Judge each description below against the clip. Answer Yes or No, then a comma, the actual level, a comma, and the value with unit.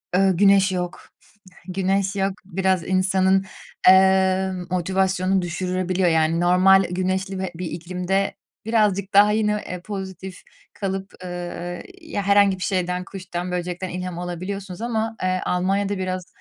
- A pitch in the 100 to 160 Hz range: No, high, 190 Hz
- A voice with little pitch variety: Yes, narrow, 1.2 semitones